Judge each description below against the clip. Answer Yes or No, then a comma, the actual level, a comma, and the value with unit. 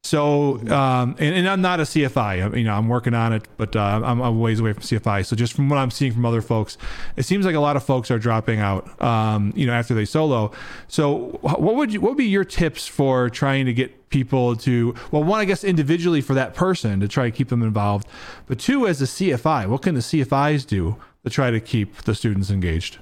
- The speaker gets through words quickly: Yes, fast, 245 wpm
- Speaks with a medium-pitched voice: No, low, 125 Hz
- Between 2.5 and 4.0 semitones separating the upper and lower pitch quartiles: No, average, 4.7 semitones